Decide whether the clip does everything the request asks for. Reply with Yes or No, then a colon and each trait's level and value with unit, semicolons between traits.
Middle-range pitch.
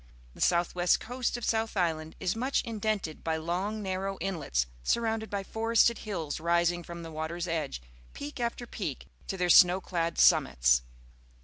Yes: medium, 180 Hz